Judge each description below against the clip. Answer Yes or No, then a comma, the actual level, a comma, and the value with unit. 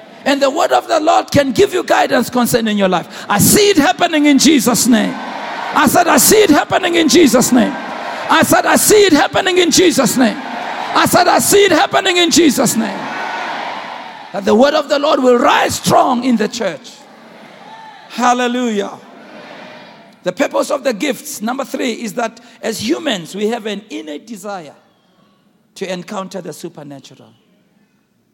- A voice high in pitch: Yes, high, 245 Hz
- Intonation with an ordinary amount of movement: No, wide, 6.0 semitones